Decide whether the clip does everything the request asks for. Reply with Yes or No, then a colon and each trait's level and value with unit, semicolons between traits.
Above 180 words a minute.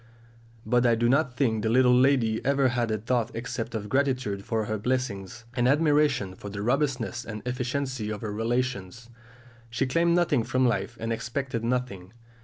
No: average, 175 wpm